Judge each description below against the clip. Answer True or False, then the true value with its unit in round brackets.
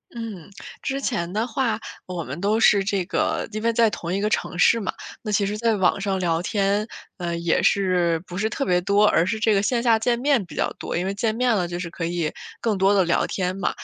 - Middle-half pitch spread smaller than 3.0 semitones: False (3.7 semitones)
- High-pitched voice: True (200 Hz)